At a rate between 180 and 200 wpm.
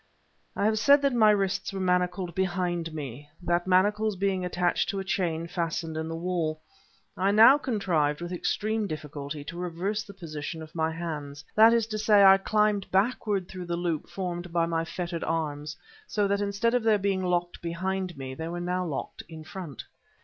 Yes: average, 190 wpm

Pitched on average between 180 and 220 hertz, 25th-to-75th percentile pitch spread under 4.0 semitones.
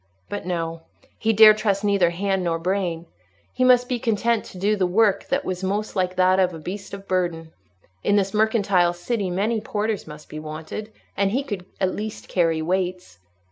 Yes: high, 190 Hz; average, 3.2 semitones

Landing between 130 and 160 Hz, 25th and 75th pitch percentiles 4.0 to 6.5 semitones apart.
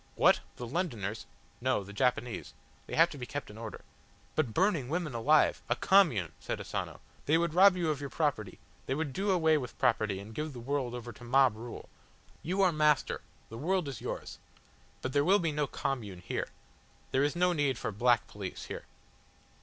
Yes: low, 135 Hz; wide, 5.4 semitones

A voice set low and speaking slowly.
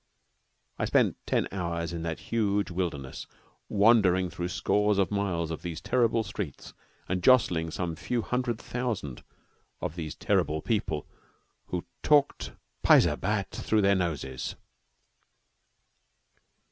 Yes: very low, 95 Hz; slow, 120 wpm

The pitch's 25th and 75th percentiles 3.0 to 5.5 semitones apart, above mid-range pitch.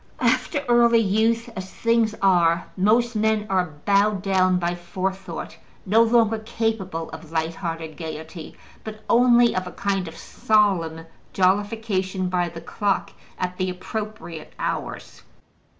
Yes: average, 3.9 semitones; high, 195 Hz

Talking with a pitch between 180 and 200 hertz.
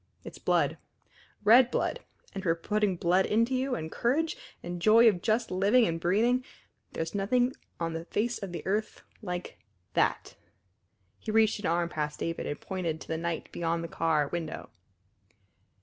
Yes: high, 190 Hz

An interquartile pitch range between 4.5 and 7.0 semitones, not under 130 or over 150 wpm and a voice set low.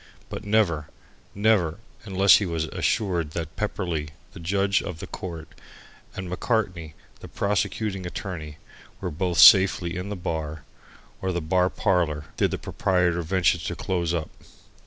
No: average, 3.2 semitones; average, 145 wpm; very low, 90 Hz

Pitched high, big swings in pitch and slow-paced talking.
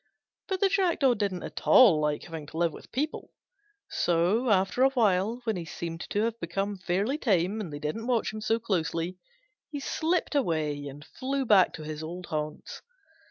No: high, 195 Hz; wide, 6.6 semitones; average, 185 wpm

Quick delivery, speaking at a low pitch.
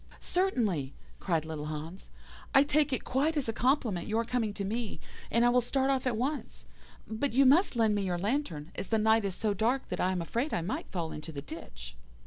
No: fast, 220 wpm; high, 220 Hz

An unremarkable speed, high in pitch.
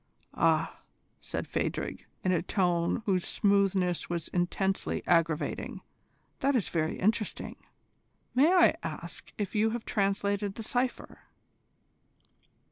No: slow, 115 wpm; high, 195 Hz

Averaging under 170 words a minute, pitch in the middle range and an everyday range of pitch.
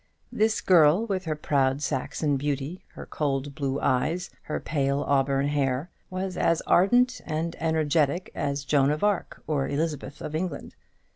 Yes: average, 150 wpm; medium, 150 Hz; average, 3.7 semitones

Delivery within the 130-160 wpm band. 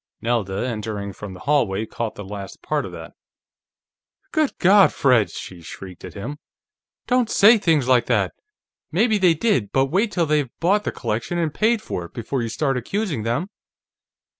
No: average, 175 wpm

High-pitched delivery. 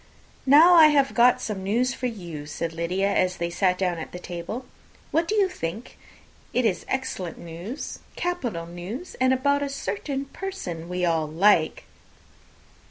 Yes: high, 200 Hz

